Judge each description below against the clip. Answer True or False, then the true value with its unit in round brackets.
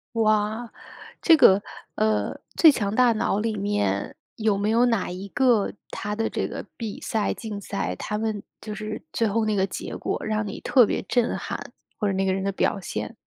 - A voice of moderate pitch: False (215 Hz)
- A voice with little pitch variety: True (2.2 semitones)